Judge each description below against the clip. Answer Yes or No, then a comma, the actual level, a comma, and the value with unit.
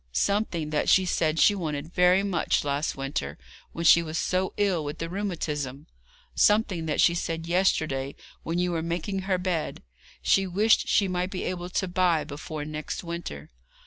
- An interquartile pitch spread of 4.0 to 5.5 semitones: No, average, 3.3 semitones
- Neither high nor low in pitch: Yes, medium, 170 Hz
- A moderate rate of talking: Yes, average, 175 wpm